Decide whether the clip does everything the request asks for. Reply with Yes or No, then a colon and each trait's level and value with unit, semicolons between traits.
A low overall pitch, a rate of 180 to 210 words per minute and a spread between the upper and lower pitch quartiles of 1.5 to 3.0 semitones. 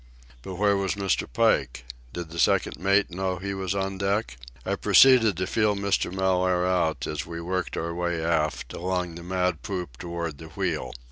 Yes: very low, 90 Hz; average, 185 wpm; narrow, 2.5 semitones